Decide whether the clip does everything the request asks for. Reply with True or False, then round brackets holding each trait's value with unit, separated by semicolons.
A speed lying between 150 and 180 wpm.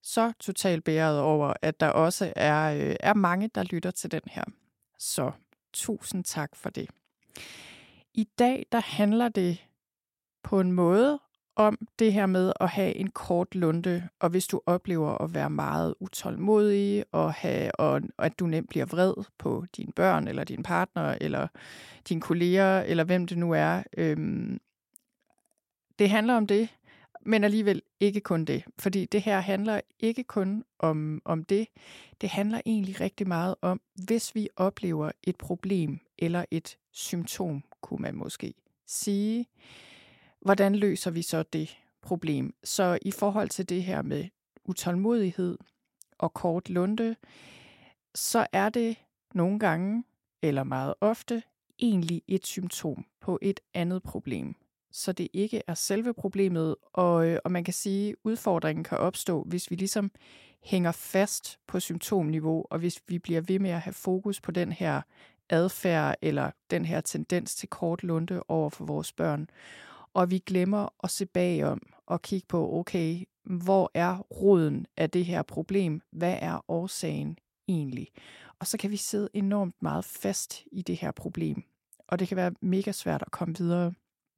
True (160 wpm)